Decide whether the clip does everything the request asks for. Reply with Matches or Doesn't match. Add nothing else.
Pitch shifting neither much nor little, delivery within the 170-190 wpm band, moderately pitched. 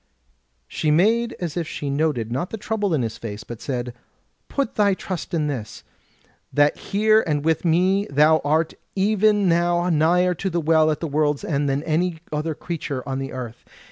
Matches